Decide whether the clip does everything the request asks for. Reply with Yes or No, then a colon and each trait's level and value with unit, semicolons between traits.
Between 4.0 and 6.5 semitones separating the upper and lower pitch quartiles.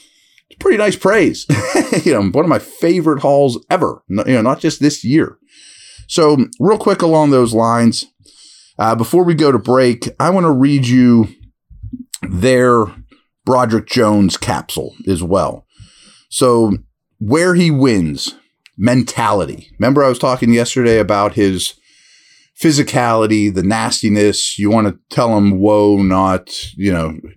Yes: average, 5.2 semitones